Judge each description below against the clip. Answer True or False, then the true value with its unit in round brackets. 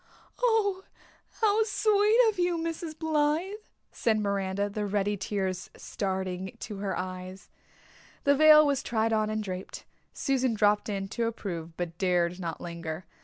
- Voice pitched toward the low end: False (210 Hz)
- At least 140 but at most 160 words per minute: True (145 wpm)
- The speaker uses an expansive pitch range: True (8.6 semitones)